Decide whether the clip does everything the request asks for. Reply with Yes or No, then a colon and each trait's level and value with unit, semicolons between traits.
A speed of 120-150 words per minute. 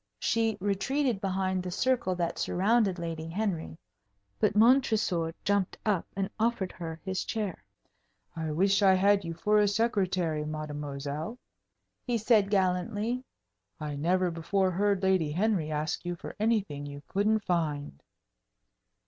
Yes: slow, 135 wpm